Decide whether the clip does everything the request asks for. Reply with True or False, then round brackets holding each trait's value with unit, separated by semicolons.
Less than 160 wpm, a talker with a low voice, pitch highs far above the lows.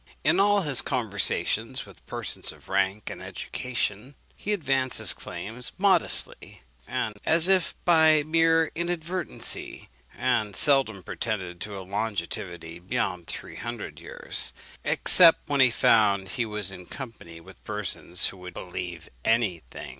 True (140 wpm; 110 Hz; 8.5 semitones)